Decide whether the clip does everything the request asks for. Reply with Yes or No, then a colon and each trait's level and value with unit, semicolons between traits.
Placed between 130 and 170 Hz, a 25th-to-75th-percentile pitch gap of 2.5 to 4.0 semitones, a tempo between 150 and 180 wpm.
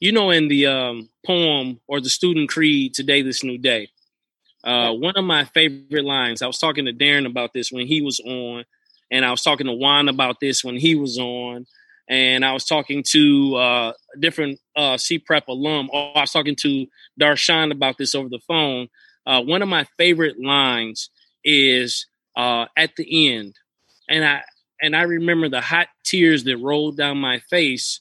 No: medium, 140 Hz; average, 3.5 semitones; average, 195 wpm